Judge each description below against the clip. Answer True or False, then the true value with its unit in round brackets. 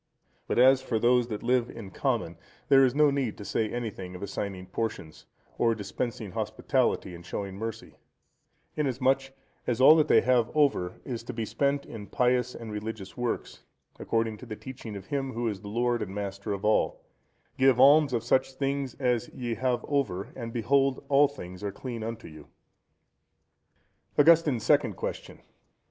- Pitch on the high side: False (120 Hz)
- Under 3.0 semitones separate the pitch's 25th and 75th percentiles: False (4.0 semitones)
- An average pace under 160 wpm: False (170 wpm)